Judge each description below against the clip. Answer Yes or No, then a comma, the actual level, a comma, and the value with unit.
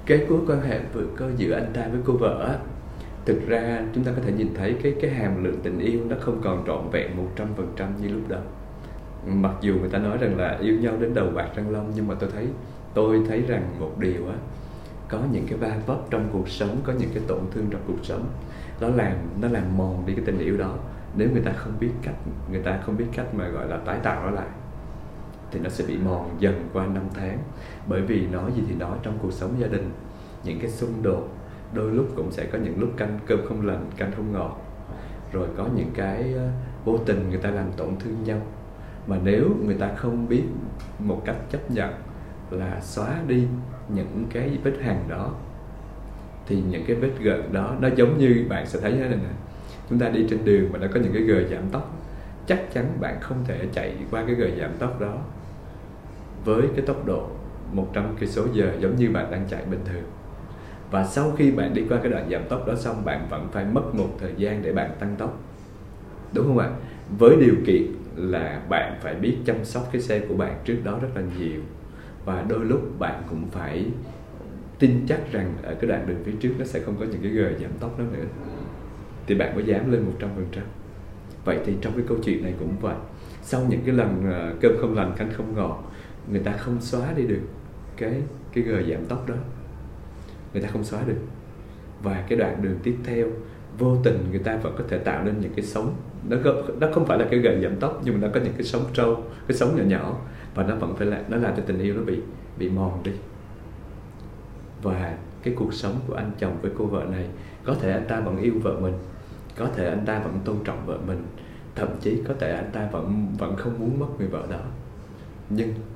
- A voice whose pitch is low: Yes, low, 105 Hz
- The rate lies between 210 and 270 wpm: Yes, average, 230 wpm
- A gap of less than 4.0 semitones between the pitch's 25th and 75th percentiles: Yes, average, 3.6 semitones